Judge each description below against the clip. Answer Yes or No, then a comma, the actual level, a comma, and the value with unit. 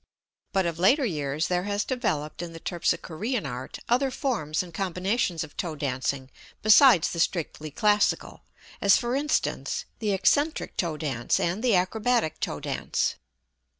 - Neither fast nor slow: Yes, average, 150 wpm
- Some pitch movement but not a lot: No, wide, 6.2 semitones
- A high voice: No, medium, 180 Hz